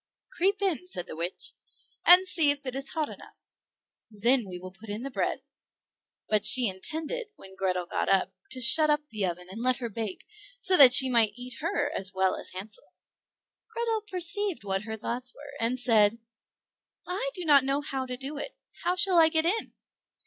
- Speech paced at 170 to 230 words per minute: Yes, average, 200 wpm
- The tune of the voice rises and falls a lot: Yes, wide, 7.6 semitones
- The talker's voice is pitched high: Yes, very high, 255 Hz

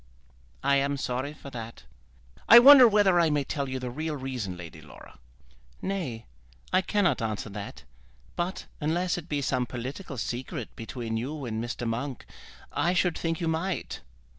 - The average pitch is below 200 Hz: Yes, medium, 140 Hz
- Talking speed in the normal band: Yes, average, 165 wpm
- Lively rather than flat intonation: Yes, wide, 6.2 semitones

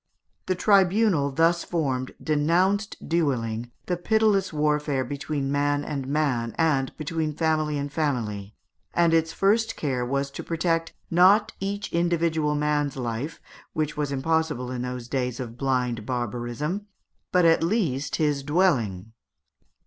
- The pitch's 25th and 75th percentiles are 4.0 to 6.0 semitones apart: Yes, average, 4.4 semitones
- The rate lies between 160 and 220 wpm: No, slow, 135 wpm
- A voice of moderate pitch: Yes, medium, 150 Hz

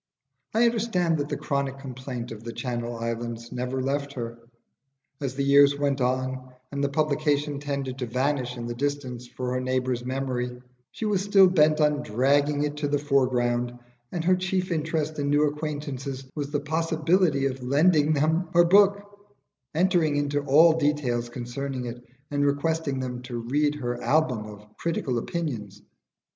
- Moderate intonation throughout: Yes, average, 3.5 semitones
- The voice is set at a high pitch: No, medium, 140 Hz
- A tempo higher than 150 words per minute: Yes, average, 165 wpm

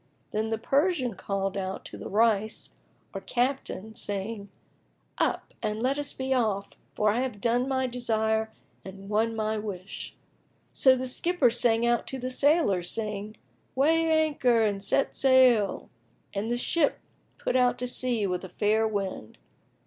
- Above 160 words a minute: No, average, 155 wpm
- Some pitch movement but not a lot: Yes, average, 3.7 semitones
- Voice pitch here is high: Yes, high, 225 Hz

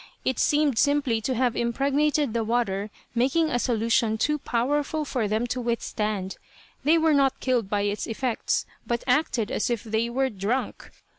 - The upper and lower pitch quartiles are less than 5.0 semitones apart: Yes, average, 3.8 semitones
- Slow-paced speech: No, average, 165 wpm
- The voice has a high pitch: Yes, high, 240 Hz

